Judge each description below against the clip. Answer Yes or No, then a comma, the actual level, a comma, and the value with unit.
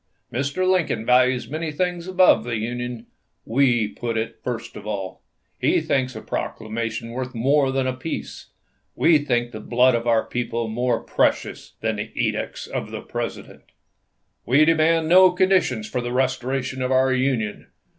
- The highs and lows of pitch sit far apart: No, average, 3.8 semitones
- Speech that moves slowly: No, average, 155 wpm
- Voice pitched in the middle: No, low, 125 Hz